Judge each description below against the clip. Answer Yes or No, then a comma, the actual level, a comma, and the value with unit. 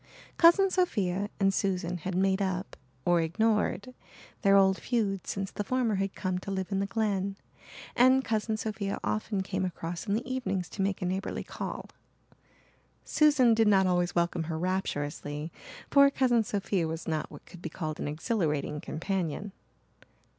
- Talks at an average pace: Yes, average, 160 wpm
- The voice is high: Yes, high, 195 Hz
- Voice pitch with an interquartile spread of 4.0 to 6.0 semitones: No, average, 3.5 semitones